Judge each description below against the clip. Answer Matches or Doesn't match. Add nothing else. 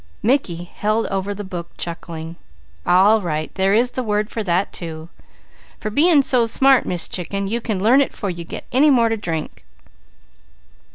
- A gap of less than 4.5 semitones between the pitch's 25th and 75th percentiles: Doesn't match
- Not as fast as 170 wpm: Doesn't match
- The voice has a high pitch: Matches